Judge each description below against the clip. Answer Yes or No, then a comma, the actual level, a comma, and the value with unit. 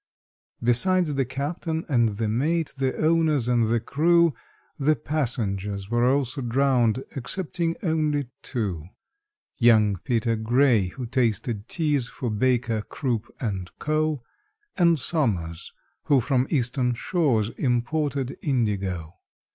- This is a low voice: Yes, low, 125 Hz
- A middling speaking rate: No, slow, 115 wpm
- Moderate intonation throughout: Yes, average, 4.9 semitones